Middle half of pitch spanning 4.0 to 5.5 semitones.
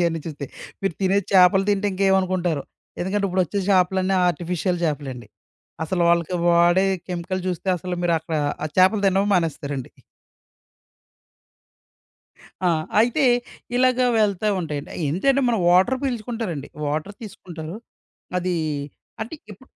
No: average, 2.8 semitones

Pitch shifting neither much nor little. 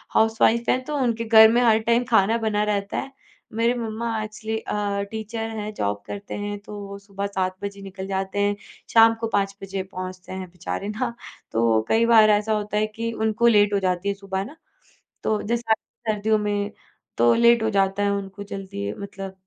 No: narrow, 2.2 semitones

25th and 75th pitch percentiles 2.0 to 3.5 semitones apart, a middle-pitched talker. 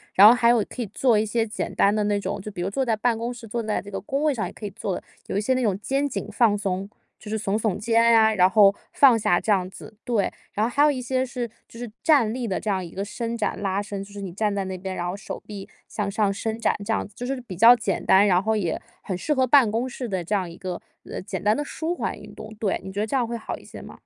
No: average, 3.2 semitones; high, 215 Hz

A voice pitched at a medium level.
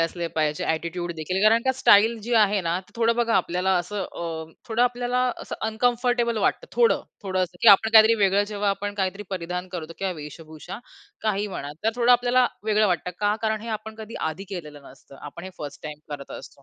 No: high, 200 Hz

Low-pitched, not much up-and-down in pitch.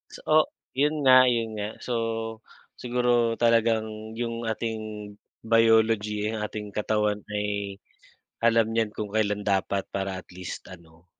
Yes: low, 110 Hz; narrow, 1.9 semitones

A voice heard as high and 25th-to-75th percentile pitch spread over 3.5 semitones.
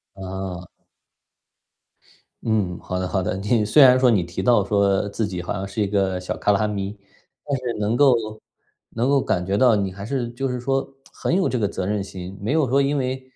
No: low, 105 Hz; average, 4.6 semitones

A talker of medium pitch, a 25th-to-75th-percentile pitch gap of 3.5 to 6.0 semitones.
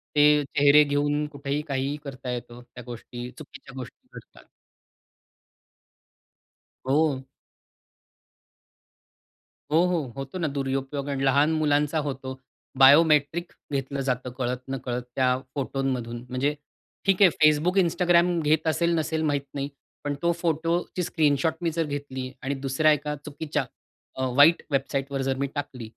No: medium, 145 Hz; average, 2.7 semitones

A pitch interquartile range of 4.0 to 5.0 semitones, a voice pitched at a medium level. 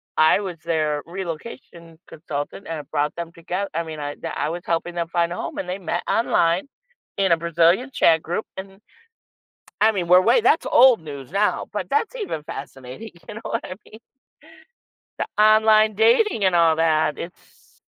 Yes: average, 4.4 semitones; medium, 170 Hz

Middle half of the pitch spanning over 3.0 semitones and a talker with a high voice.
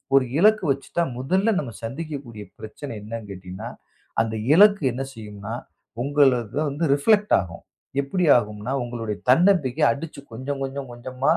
No: average, 5.1 semitones; low, 135 Hz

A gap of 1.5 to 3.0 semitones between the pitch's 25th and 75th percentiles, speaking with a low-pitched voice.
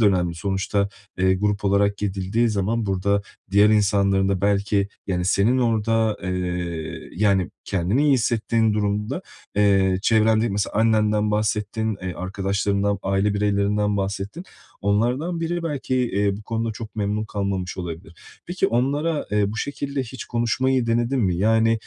Yes: narrow, 2.6 semitones; low, 105 Hz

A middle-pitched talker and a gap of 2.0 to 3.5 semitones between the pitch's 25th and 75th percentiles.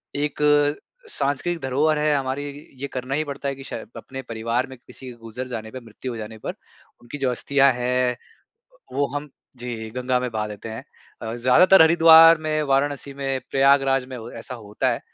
No: low, 130 Hz; average, 2.9 semitones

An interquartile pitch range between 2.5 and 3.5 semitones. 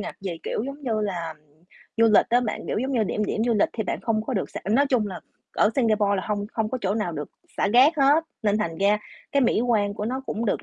Yes: average, 3.2 semitones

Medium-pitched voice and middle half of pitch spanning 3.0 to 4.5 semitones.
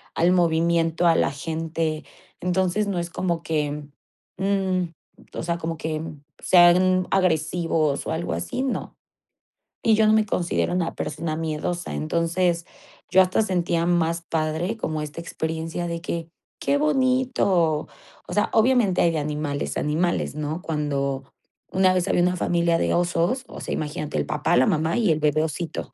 No: medium, 170 Hz; narrow, 2.6 semitones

